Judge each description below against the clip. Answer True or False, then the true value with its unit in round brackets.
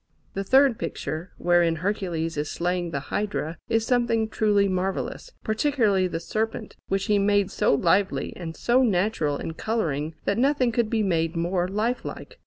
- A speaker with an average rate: True (165 wpm)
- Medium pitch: False (195 Hz)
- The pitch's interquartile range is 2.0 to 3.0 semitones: False (4.7 semitones)